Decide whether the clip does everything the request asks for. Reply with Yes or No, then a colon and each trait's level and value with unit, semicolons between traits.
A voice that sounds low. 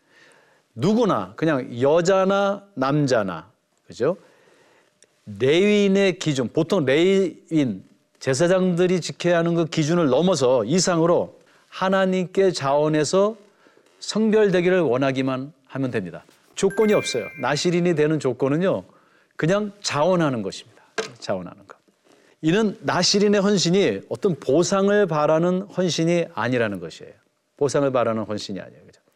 No: medium, 175 Hz